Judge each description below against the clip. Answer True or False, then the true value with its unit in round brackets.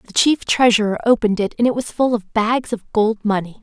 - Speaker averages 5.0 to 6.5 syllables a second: True (5.5 syllables/s)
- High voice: True (225 Hz)